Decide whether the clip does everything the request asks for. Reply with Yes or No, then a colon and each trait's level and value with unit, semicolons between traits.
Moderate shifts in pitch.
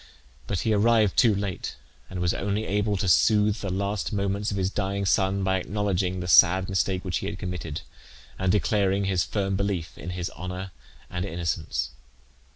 No: narrow, 2.0 semitones